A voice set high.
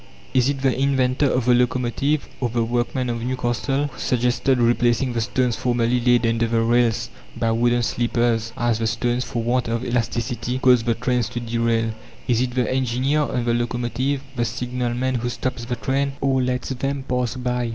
No: low, 120 Hz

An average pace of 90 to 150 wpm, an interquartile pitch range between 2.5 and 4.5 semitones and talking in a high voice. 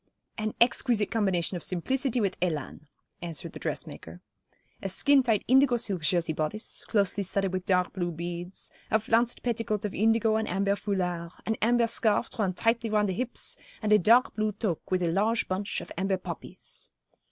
No: average, 175 wpm; average, 3.9 semitones; high, 205 Hz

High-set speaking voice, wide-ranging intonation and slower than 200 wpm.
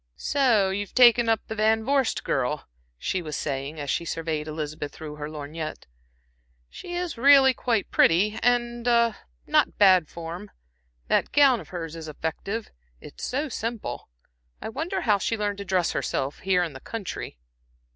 Yes: high, 200 Hz; wide, 6.9 semitones; average, 165 wpm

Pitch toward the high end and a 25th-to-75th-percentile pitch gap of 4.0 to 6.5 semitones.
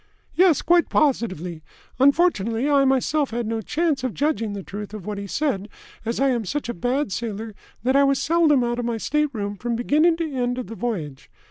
Yes: high, 245 Hz; average, 5.1 semitones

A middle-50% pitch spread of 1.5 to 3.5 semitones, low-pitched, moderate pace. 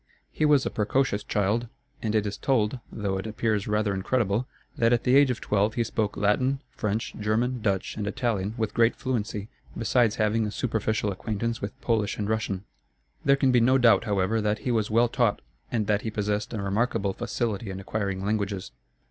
Yes: narrow, 2.4 semitones; low, 110 Hz; average, 190 wpm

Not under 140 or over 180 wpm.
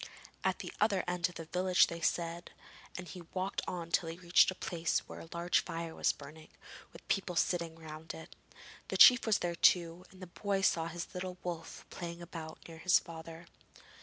No: average, 195 wpm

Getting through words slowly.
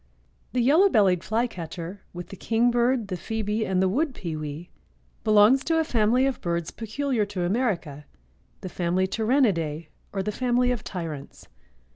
No: average, 150 wpm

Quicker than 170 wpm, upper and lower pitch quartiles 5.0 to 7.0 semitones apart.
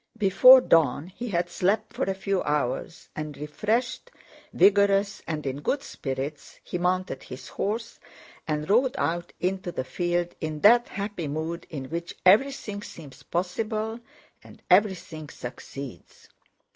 No: slow, 135 wpm; average, 5.3 semitones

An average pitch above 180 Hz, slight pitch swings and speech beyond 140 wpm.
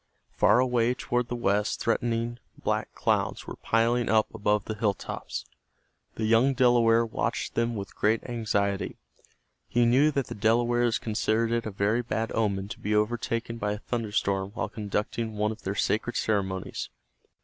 No: low, 115 Hz; narrow, 2.2 semitones; average, 165 wpm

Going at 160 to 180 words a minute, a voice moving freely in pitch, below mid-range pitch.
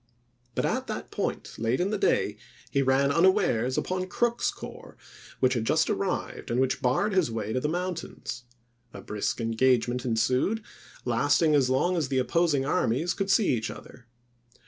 Yes: average, 170 wpm; wide, 6.3 semitones; low, 130 Hz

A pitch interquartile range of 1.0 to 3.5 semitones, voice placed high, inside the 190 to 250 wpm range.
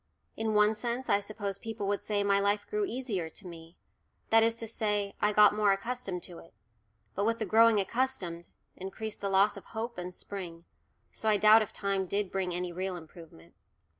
Yes: average, 2.9 semitones; high, 205 Hz; average, 195 wpm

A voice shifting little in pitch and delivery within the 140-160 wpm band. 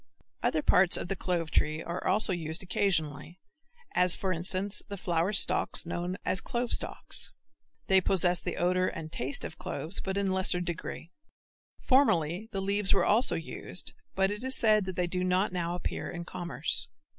No: narrow, 2.3 semitones; average, 180 wpm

